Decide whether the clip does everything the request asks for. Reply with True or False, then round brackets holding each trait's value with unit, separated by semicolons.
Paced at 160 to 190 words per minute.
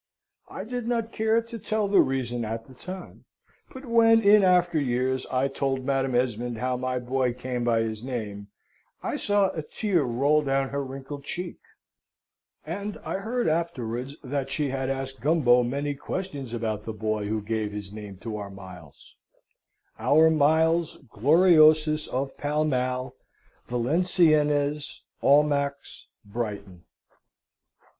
False (140 wpm)